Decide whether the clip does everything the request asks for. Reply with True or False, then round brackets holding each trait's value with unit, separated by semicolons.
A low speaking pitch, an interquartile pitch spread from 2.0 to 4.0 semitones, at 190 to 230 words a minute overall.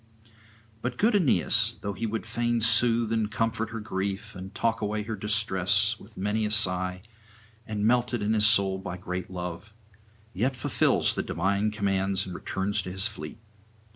False (105 Hz; 2.9 semitones; 170 wpm)